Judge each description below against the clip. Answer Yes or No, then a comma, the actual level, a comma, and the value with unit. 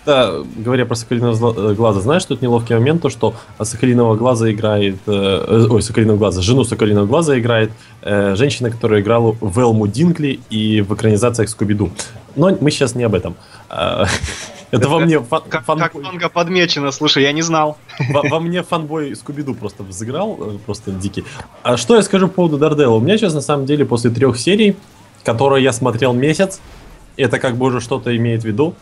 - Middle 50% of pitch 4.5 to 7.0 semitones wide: Yes, average, 5.2 semitones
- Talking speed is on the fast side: Yes, fast, 175 wpm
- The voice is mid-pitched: No, low, 125 Hz